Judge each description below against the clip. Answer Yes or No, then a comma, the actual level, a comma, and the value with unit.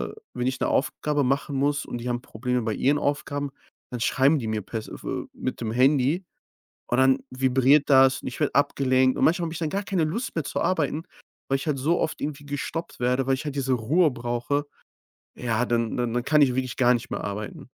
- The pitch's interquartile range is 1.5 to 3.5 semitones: Yes, average, 2.9 semitones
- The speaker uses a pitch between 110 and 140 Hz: Yes, low, 135 Hz